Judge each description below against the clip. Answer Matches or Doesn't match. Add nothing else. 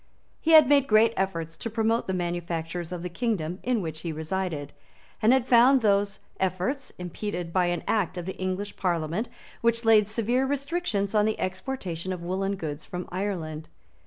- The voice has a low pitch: Doesn't match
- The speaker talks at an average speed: Matches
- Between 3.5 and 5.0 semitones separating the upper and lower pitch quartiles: Matches